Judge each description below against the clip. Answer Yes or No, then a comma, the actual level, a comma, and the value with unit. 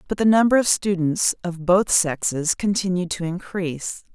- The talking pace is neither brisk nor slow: Yes, average, 160 wpm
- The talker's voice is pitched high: No, medium, 180 Hz